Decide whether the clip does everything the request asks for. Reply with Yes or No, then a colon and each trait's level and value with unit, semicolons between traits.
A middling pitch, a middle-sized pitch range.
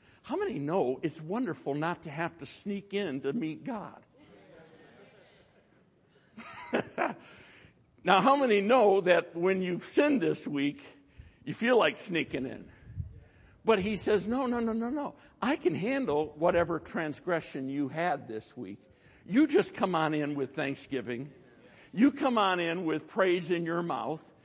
No: medium, 170 Hz; wide, 6.1 semitones